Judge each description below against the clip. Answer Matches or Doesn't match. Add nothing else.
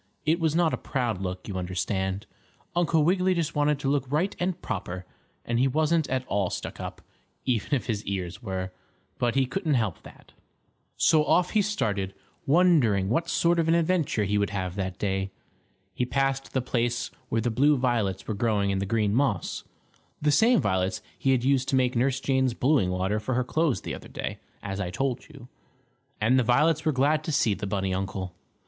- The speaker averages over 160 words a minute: Matches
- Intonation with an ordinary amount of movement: Doesn't match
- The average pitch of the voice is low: Matches